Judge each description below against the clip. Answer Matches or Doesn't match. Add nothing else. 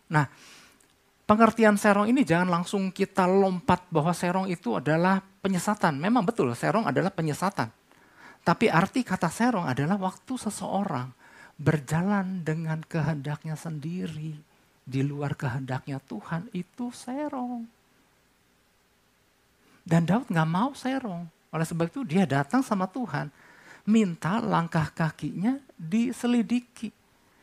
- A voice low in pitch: Doesn't match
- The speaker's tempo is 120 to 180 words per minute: Doesn't match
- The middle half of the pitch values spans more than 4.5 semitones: Matches